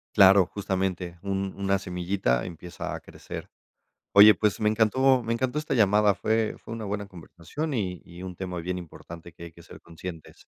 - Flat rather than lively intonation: No, average, 3.3 semitones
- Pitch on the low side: Yes, very low, 95 Hz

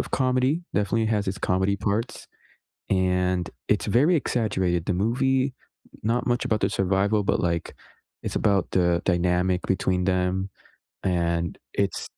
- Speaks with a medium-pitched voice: No, very low, 95 Hz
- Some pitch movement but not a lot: Yes, average, 3.7 semitones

